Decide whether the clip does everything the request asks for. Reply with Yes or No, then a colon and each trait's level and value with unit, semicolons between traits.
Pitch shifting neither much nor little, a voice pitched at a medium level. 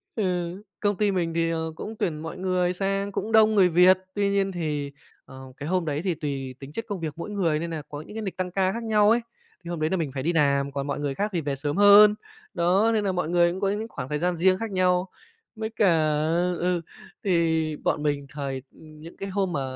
Yes: average, 4.3 semitones; medium, 175 Hz